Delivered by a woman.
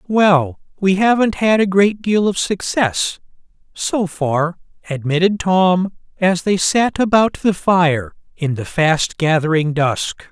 No: male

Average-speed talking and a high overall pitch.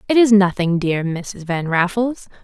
Yes: average, 175 wpm; high, 195 Hz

